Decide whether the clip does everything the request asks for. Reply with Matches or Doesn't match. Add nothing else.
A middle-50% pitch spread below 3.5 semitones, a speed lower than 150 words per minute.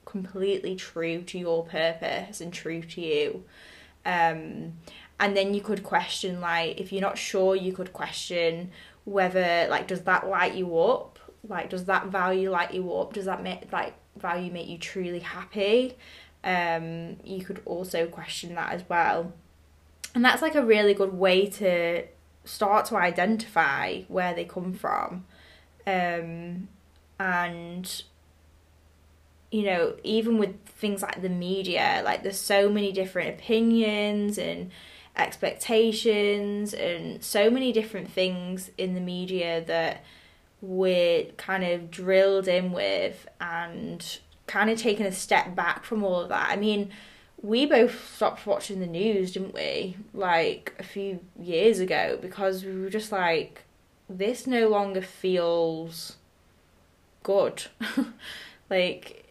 Matches